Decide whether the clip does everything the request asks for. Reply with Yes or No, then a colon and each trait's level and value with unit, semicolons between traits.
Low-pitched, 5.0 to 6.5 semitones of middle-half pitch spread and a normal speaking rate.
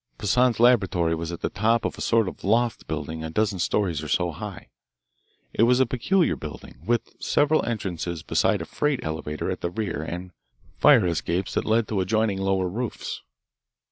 Yes: very low, 95 Hz; wide, 5.4 semitones; average, 180 wpm